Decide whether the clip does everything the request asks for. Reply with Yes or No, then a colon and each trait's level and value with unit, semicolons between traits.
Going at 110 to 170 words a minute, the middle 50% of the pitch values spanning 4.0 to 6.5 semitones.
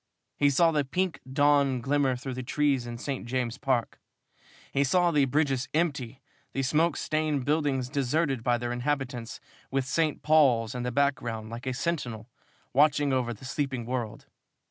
No: average, 165 wpm; average, 3.0 semitones